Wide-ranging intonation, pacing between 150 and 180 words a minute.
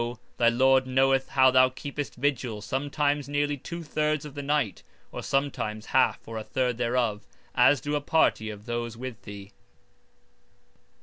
No: average, 3.5 semitones; average, 160 wpm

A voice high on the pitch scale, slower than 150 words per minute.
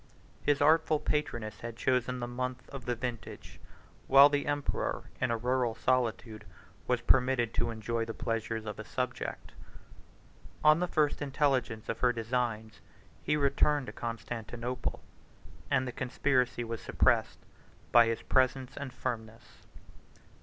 No: low, 125 Hz; average, 140 wpm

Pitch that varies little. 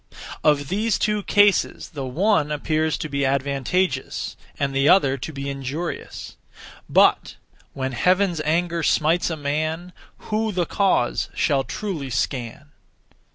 No: average, 4.6 semitones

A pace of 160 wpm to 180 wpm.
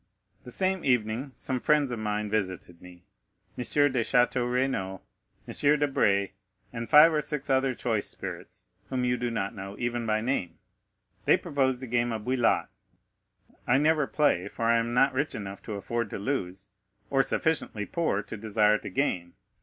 Yes: average, 170 wpm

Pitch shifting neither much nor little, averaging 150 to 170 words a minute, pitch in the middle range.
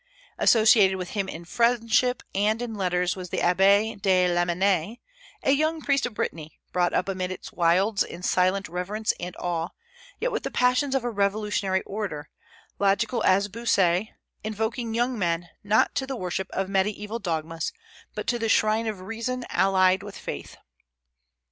No: average, 3.7 semitones; average, 160 wpm; high, 200 Hz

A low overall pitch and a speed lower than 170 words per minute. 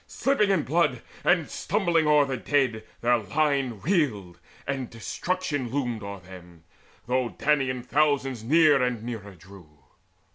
Yes: low, 130 Hz; average, 140 wpm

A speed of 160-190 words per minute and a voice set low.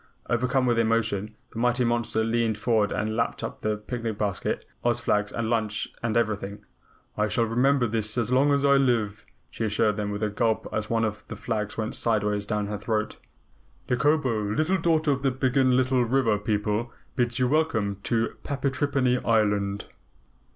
Yes: average, 170 wpm; low, 115 Hz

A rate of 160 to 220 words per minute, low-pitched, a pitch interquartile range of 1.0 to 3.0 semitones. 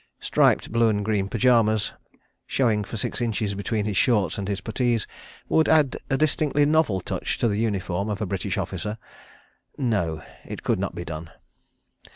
No: average, 170 wpm; low, 105 Hz; average, 3.4 semitones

